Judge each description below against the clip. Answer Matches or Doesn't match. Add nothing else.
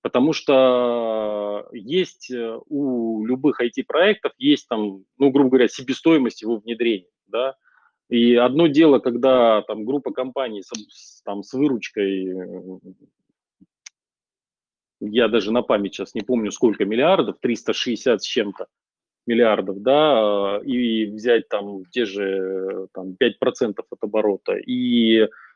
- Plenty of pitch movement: Doesn't match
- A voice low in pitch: Matches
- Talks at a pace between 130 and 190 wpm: Doesn't match